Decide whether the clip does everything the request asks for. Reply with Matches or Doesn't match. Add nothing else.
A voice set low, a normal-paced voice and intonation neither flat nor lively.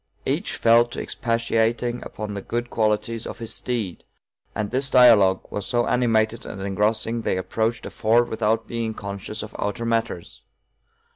Doesn't match